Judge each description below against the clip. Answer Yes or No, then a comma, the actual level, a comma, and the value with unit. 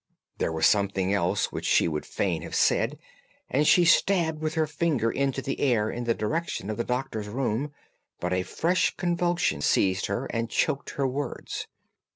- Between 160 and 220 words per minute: Yes, average, 180 wpm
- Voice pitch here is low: Yes, low, 125 Hz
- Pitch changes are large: Yes, wide, 7.2 semitones